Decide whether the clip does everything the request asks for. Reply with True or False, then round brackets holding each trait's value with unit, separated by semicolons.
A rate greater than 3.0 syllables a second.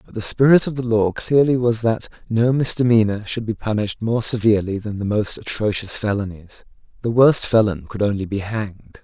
True (5.5 syllables/s)